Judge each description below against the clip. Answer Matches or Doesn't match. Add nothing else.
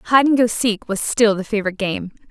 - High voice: Matches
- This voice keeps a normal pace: Doesn't match